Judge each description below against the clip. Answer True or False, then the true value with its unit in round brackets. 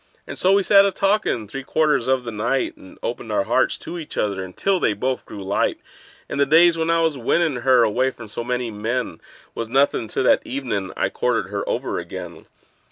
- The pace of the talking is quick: True (215 wpm)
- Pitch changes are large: True (6.6 semitones)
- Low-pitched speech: True (130 Hz)